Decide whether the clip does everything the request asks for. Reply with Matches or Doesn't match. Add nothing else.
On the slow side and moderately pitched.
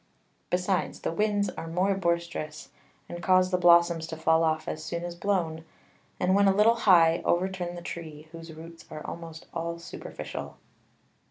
Doesn't match